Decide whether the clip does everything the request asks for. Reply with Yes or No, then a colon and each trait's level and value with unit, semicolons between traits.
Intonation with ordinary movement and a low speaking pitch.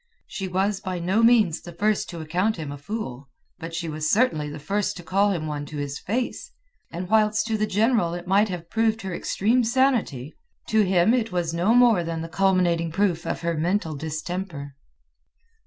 No: average, 4.6 semitones; medium, 185 Hz